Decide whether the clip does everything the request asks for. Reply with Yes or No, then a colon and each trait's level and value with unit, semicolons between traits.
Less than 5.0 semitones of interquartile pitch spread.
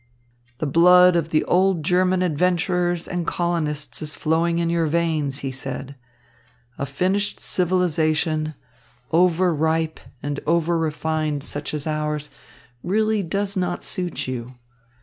Yes: average, 2.8 semitones